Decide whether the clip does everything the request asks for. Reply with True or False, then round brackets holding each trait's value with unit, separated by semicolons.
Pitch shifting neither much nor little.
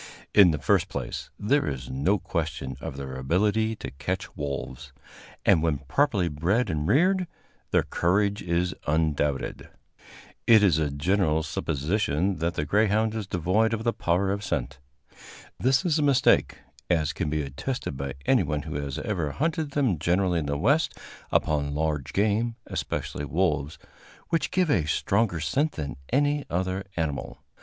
False (6.8 semitones)